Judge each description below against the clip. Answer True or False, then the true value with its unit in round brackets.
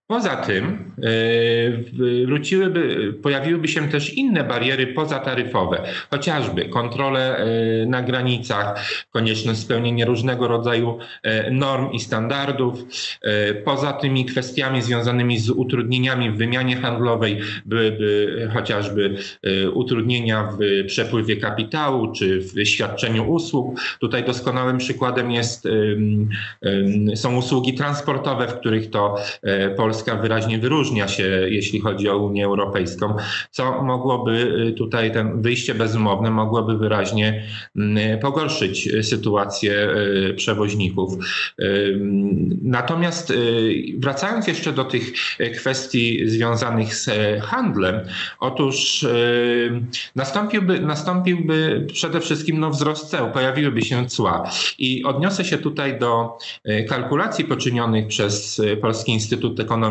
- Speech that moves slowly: True (100 wpm)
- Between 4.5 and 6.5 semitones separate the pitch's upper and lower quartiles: False (3.4 semitones)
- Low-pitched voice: True (120 Hz)